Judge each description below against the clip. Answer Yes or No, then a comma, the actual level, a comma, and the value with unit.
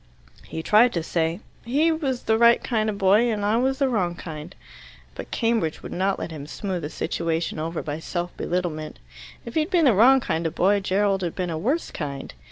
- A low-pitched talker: No, high, 195 Hz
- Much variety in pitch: Yes, wide, 6.1 semitones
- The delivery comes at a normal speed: No, fast, 215 wpm